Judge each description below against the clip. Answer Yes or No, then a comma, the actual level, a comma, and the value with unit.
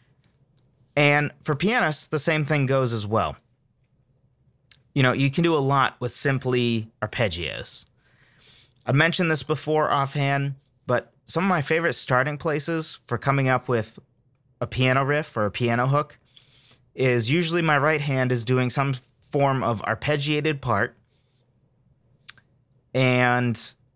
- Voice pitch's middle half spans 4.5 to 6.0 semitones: No, narrow, 2.6 semitones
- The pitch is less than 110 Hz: No, low, 130 Hz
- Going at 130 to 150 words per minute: Yes, average, 140 wpm